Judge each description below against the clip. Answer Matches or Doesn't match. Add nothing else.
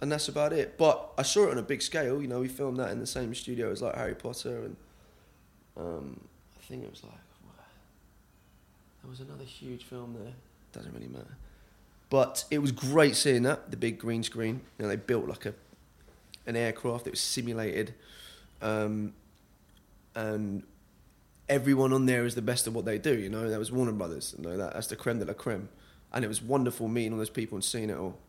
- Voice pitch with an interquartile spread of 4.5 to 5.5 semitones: Doesn't match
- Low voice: Matches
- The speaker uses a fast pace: Matches